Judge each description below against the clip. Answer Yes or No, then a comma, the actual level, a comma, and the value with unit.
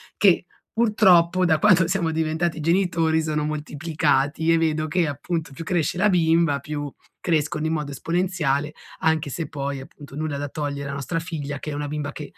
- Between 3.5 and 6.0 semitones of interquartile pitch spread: No, narrow, 2.6 semitones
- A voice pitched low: No, medium, 155 Hz